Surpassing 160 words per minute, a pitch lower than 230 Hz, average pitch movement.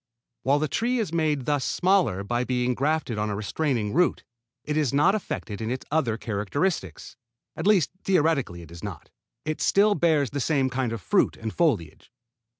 No: average, 180 wpm; medium, 140 Hz; wide, 6.3 semitones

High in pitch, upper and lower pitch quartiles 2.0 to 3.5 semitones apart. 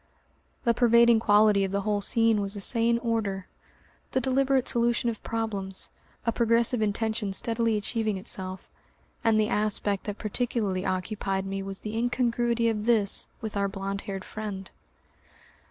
Yes: high, 215 Hz; average, 2.8 semitones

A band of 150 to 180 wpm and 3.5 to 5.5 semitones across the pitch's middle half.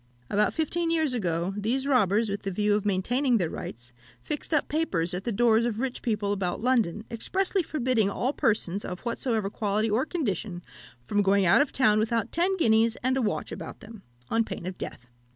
No: average, 195 wpm; average, 4.5 semitones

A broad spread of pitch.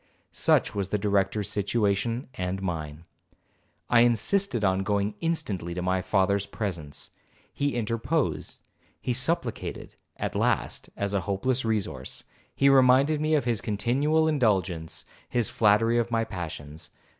No: average, 4.7 semitones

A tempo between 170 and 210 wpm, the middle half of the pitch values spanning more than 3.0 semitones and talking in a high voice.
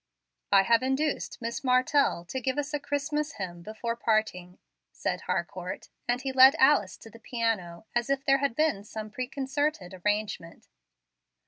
No: average, 155 wpm; average, 4.8 semitones; high, 240 Hz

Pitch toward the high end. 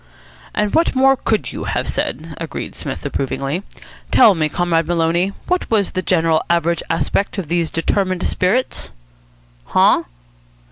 No: medium, 175 Hz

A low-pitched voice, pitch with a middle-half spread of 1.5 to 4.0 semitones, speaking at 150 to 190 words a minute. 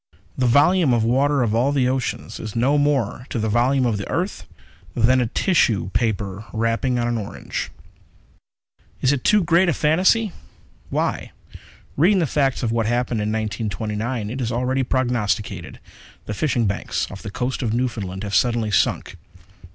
Yes: low, 120 Hz; average, 3.6 semitones; average, 165 wpm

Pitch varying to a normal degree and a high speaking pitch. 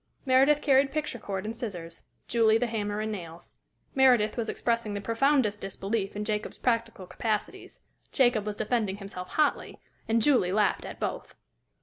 Yes: average, 3.3 semitones; high, 220 Hz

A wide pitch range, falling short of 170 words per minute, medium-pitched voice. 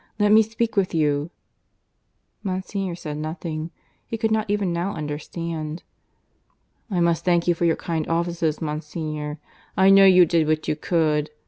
No: average, 3.5 semitones; average, 155 wpm; medium, 170 Hz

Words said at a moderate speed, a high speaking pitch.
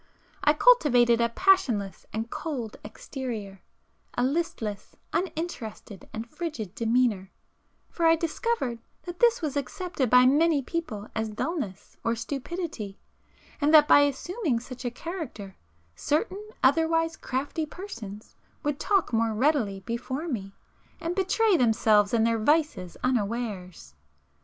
No: slow, 120 wpm; very high, 255 Hz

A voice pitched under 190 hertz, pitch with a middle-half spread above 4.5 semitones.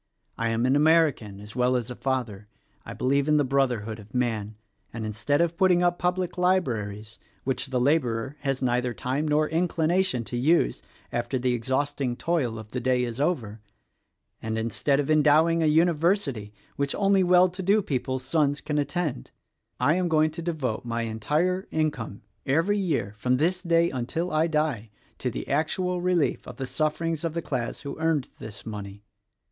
Yes: medium, 140 Hz; wide, 5.5 semitones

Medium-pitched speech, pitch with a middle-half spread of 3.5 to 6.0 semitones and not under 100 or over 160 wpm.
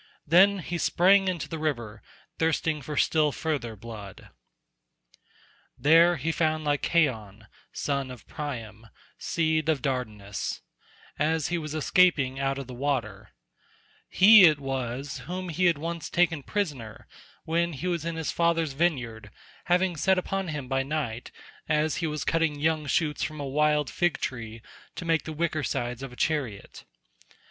Yes: medium, 150 Hz; average, 4.2 semitones; average, 155 wpm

